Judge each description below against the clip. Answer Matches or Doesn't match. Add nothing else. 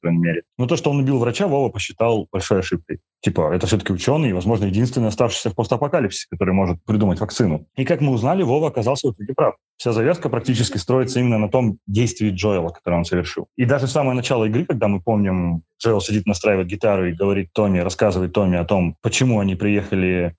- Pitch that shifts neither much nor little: Matches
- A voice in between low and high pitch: Doesn't match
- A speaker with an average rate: Doesn't match